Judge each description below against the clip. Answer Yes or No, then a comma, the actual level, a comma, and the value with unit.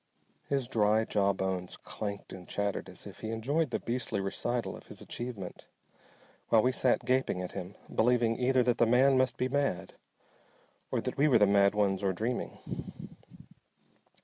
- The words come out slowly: No, average, 170 wpm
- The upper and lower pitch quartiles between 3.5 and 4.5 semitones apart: Yes, average, 4.0 semitones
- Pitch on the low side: Yes, low, 115 Hz